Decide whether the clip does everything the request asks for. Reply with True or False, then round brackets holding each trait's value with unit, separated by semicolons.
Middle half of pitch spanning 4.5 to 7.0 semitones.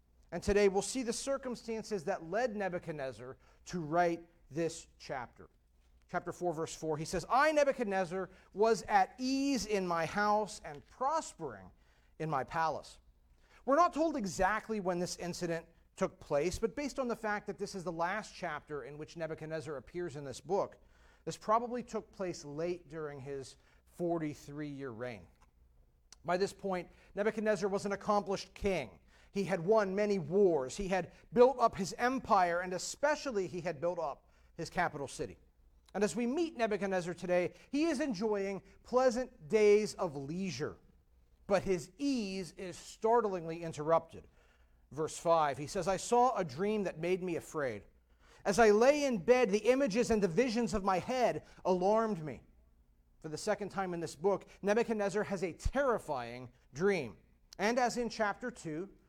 True (5.5 semitones)